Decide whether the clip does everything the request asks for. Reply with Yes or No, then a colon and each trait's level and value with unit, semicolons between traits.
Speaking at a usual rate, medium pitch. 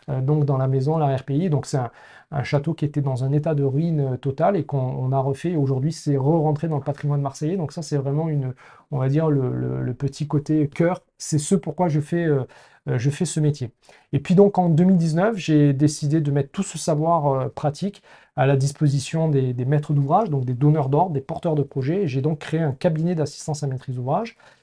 No: fast, 230 wpm; medium, 150 Hz